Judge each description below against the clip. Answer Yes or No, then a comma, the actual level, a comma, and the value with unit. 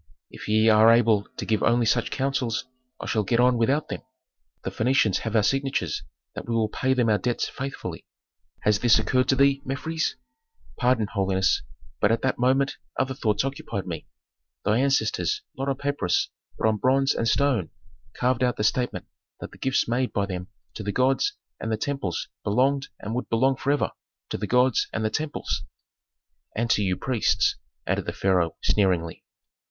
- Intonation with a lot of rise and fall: No, average, 4.0 semitones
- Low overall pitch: Yes, low, 120 Hz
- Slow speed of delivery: No, average, 180 wpm